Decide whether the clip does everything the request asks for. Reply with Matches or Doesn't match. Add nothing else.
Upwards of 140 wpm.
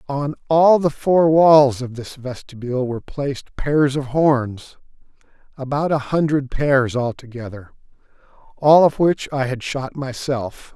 Doesn't match